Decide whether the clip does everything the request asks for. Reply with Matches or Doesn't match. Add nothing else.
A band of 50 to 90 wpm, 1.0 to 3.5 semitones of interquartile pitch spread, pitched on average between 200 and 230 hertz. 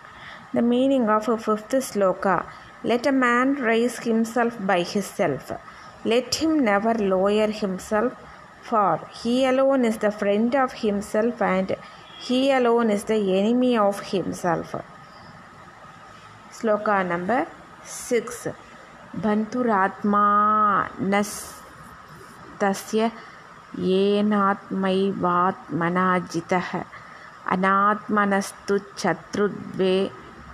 Matches